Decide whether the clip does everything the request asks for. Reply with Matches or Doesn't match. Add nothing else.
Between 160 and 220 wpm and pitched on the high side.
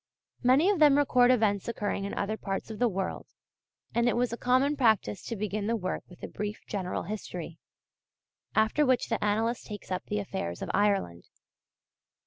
Matches